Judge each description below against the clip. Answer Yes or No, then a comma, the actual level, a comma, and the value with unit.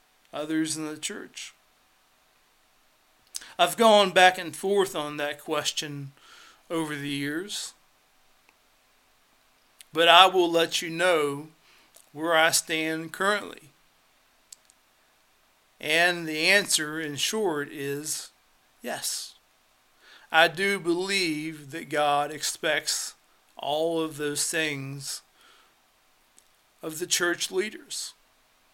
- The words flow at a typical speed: No, slow, 95 wpm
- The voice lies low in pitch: No, medium, 160 Hz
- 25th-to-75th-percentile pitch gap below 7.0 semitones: Yes, average, 2.9 semitones